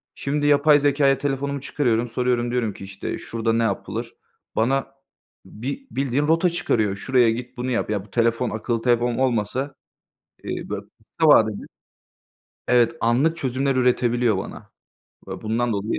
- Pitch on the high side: No, low, 125 Hz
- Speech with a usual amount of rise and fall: Yes, average, 3.3 semitones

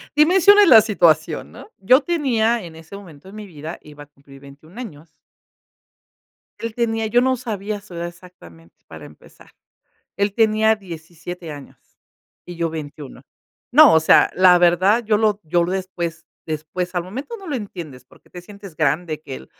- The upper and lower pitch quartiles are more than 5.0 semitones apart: Yes, wide, 5.6 semitones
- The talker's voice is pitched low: No, medium, 180 Hz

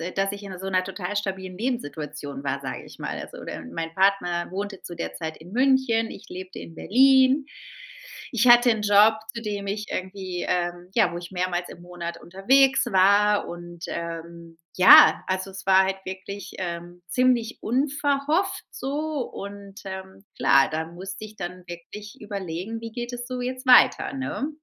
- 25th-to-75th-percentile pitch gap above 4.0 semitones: Yes, average, 4.9 semitones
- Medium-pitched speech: No, high, 195 Hz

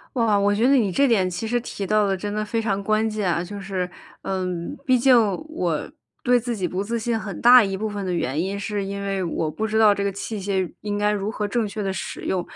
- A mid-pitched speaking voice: No, high, 205 Hz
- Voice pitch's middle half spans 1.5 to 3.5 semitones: Yes, narrow, 2.4 semitones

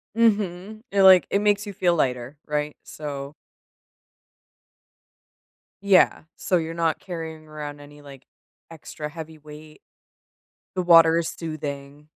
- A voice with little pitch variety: No, average, 3.4 semitones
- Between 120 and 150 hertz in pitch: No, medium, 160 Hz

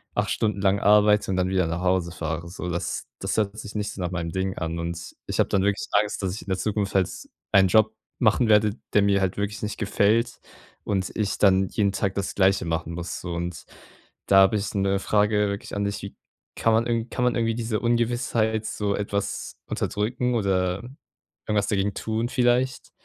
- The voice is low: Yes, low, 100 Hz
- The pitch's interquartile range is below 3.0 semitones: Yes, narrow, 2.5 semitones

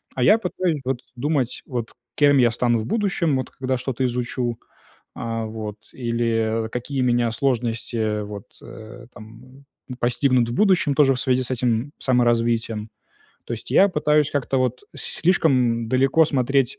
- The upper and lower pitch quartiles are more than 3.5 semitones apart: No, average, 2.9 semitones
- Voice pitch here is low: Yes, low, 125 Hz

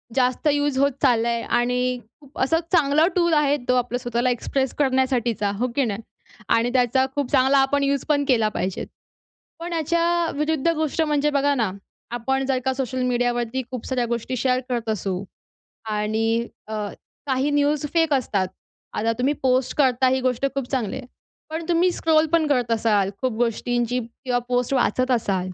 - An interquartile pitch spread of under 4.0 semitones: Yes, average, 3.2 semitones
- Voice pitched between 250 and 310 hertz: Yes, very high, 255 Hz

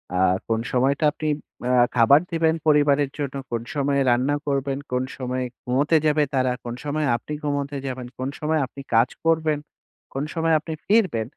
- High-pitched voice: No, medium, 140 Hz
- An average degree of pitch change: Yes, average, 3.0 semitones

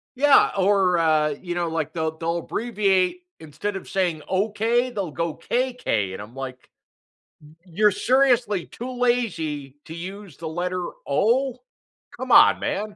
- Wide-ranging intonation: Yes, wide, 5.7 semitones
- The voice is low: No, medium, 185 Hz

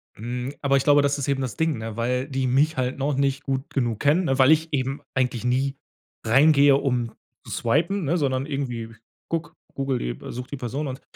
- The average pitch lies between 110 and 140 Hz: Yes, low, 135 Hz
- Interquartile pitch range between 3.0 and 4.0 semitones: No, narrow, 2.4 semitones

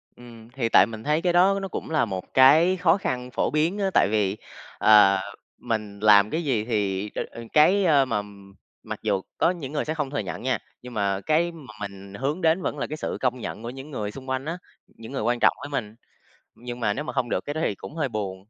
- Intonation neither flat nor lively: No, wide, 6.3 semitones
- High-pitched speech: No, low, 125 Hz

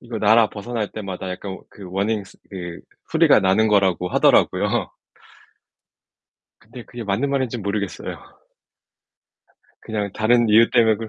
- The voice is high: No, low, 105 Hz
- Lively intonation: No, average, 2.7 semitones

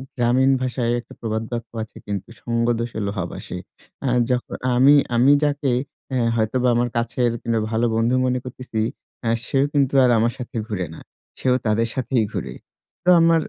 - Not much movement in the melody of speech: Yes, narrow, 2.1 semitones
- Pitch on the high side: No, low, 120 Hz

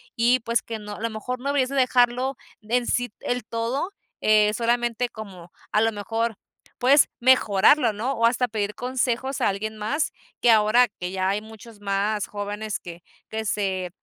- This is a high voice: Yes, high, 225 Hz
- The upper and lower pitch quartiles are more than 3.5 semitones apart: No, average, 2.9 semitones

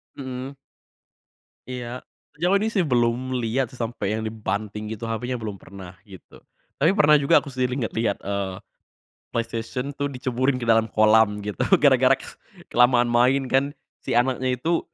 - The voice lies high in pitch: No, low, 120 Hz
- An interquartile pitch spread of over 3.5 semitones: No, average, 3.0 semitones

